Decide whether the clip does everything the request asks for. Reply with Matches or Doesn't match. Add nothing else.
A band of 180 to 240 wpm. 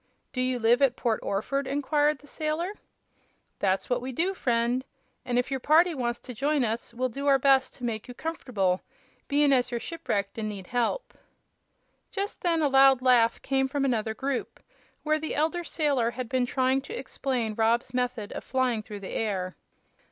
Matches